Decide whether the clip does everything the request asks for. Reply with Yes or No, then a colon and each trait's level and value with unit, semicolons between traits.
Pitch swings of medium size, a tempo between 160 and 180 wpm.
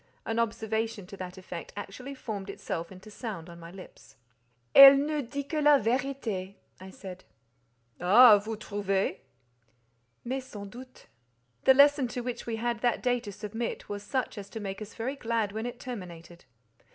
Yes: average, 4.2 semitones; average, 170 wpm